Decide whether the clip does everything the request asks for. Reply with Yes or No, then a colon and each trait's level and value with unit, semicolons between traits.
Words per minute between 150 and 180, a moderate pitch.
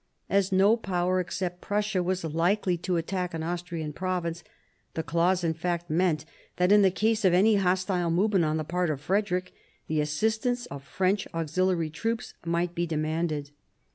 Yes: average, 170 wpm; medium, 180 Hz